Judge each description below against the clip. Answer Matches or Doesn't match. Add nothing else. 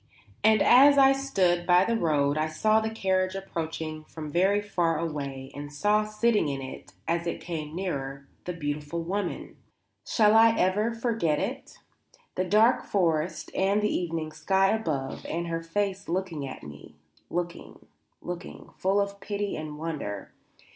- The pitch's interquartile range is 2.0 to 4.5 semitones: Doesn't match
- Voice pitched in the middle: Matches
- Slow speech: Doesn't match